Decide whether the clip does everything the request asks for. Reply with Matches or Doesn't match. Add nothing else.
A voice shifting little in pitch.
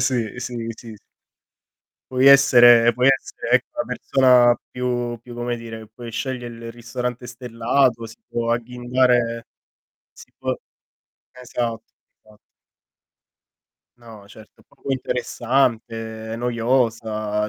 Matches